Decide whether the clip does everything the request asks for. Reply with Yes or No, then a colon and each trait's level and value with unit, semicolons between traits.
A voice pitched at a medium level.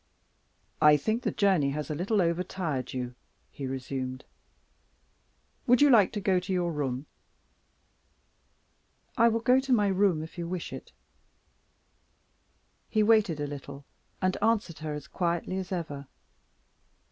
Yes: medium, 175 Hz